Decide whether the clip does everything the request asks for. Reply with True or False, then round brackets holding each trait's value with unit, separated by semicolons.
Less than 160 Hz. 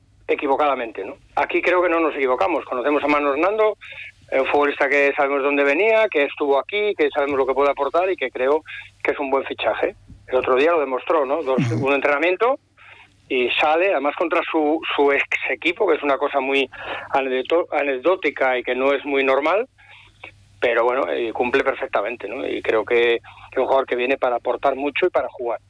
True (140 Hz)